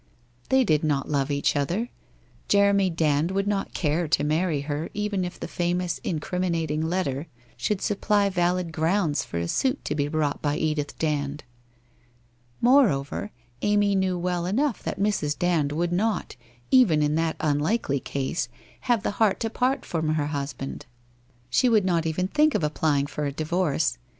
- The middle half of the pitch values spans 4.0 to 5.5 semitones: Yes, average, 5.1 semitones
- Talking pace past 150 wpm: Yes, average, 165 wpm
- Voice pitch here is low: No, medium, 170 Hz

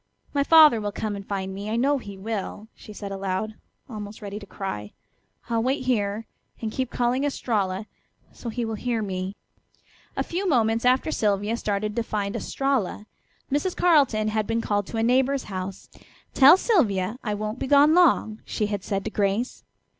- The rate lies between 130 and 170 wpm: No, average, 180 wpm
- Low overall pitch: No, high, 220 Hz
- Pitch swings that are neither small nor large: Yes, average, 4.1 semitones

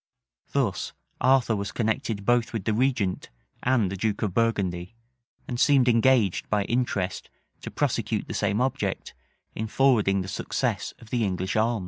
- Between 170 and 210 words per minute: No, average, 155 wpm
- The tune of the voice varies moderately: Yes, average, 3.7 semitones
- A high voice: No, low, 110 Hz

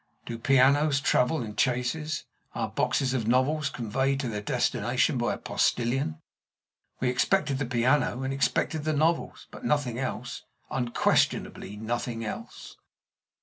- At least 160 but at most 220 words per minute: No, slow, 135 wpm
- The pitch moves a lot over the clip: No, average, 3.2 semitones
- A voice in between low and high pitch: No, low, 130 Hz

